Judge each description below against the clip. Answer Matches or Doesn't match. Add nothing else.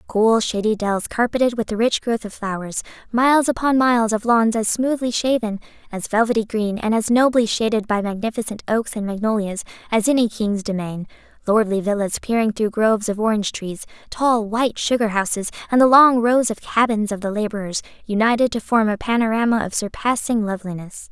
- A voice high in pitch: Matches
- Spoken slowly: Doesn't match